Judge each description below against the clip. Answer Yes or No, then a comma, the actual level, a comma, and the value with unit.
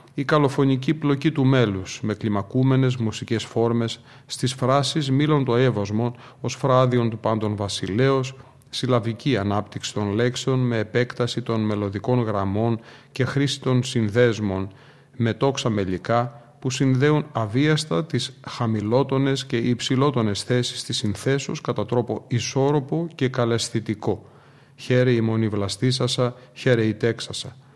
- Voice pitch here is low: Yes, low, 125 Hz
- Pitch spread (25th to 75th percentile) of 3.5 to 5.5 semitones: No, average, 2.9 semitones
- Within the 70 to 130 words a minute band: Yes, average, 120 wpm